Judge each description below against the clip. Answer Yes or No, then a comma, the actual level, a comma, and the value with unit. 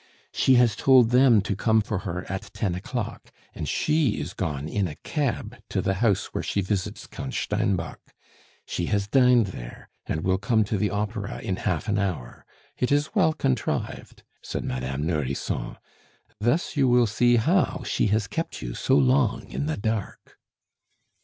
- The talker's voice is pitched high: No, low, 105 Hz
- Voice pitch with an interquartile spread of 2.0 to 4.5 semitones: No, average, 5.1 semitones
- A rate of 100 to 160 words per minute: No, average, 170 wpm